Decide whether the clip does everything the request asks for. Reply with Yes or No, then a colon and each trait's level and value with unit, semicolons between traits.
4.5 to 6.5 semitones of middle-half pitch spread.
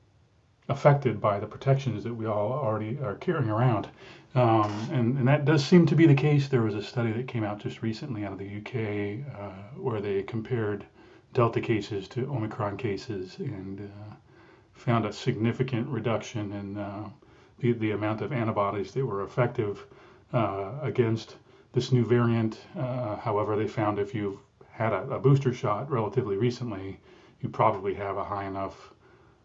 No: average, 3.6 semitones